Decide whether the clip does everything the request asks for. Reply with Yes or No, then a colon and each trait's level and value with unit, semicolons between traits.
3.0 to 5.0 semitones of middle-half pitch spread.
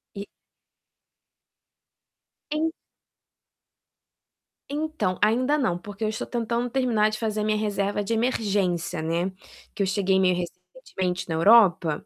Yes: average, 4.1 semitones